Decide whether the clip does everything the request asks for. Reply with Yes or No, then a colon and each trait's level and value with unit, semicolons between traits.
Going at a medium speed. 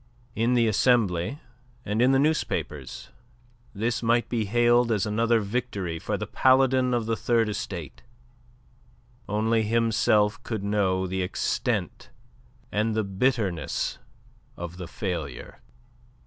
No: slow, 120 wpm